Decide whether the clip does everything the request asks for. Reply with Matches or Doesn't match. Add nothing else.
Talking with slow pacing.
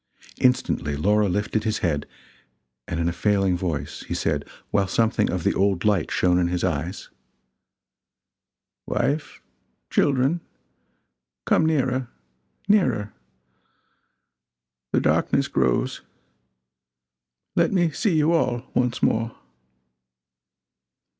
Matches